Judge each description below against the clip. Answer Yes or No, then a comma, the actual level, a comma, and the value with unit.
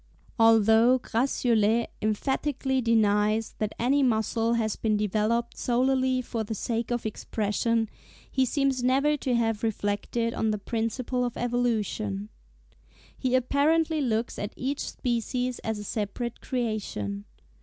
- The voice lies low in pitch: No, high, 230 Hz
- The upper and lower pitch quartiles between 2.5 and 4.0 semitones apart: Yes, average, 2.8 semitones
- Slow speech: Yes, slow, 125 wpm